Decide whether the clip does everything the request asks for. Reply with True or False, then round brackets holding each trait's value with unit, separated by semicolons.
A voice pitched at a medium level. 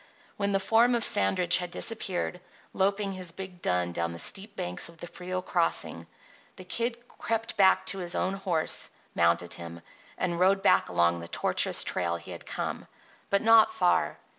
True (180 Hz)